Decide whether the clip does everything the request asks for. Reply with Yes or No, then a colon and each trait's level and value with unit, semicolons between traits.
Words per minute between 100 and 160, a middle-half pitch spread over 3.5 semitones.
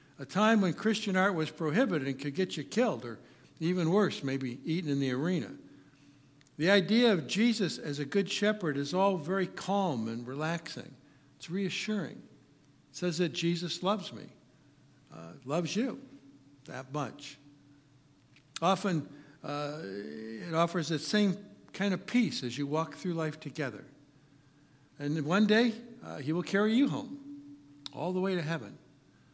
Yes: average, 155 wpm; wide, 5.4 semitones